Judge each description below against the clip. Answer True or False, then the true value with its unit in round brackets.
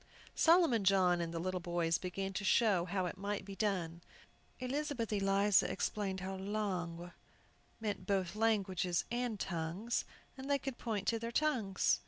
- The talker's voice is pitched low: False (195 Hz)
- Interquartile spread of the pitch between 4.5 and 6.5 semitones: False (3.7 semitones)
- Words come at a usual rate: True (155 wpm)